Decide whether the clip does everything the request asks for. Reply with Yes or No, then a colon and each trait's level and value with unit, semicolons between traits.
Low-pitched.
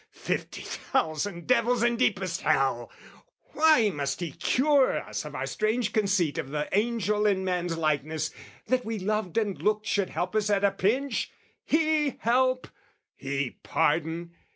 No: high, 205 Hz